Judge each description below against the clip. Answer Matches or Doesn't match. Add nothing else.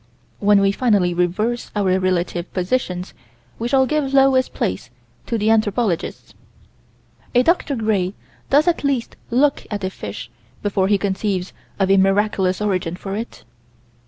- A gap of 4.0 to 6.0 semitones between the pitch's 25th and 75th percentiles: Matches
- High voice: Matches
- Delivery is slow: Doesn't match